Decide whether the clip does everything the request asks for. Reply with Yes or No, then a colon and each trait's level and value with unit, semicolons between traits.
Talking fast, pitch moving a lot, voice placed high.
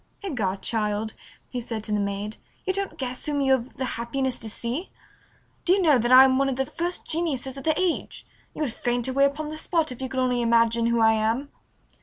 No: fast, 230 wpm; average, 3.9 semitones; very high, 255 Hz